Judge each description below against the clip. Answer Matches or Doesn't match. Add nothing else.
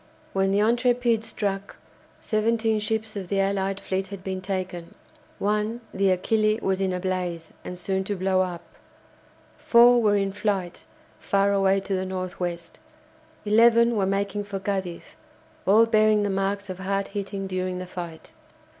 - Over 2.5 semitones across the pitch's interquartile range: Doesn't match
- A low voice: Doesn't match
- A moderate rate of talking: Matches